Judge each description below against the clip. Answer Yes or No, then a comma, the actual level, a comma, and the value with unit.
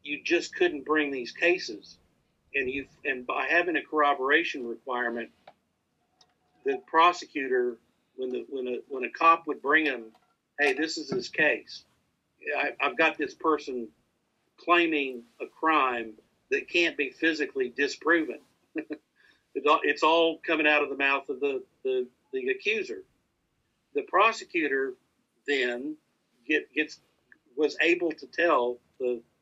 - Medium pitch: Yes, medium, 160 Hz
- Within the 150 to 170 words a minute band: No, slow, 135 wpm